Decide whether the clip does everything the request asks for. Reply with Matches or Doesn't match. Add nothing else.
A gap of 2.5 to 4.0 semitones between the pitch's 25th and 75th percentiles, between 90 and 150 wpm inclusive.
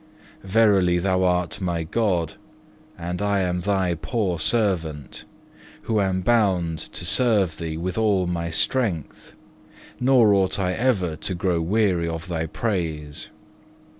Matches